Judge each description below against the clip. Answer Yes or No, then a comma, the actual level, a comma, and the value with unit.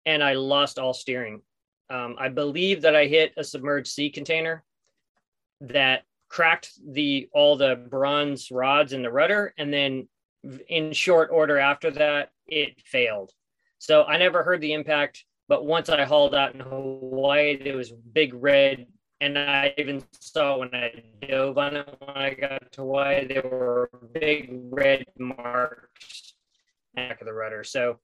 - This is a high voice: No, medium, 140 Hz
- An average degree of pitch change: No, narrow, 2.2 semitones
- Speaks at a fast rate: No, average, 160 wpm